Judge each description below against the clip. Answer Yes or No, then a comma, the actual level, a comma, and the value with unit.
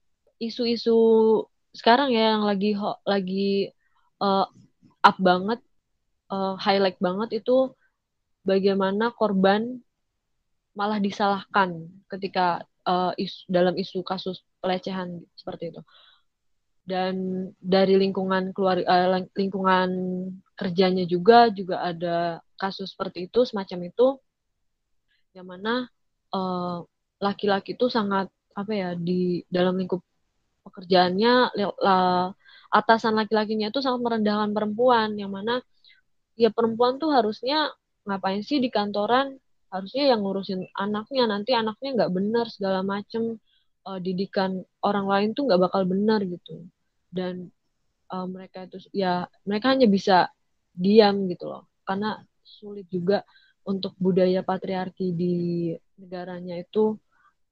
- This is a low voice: No, high, 195 Hz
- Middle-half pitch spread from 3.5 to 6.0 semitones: No, average, 2.9 semitones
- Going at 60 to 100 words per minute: No, average, 115 wpm